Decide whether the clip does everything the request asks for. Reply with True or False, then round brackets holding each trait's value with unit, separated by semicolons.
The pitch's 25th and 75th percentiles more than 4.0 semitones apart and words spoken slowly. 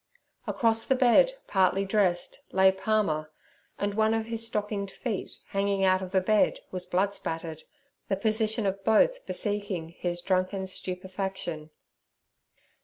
False (2.7 semitones; 130 wpm)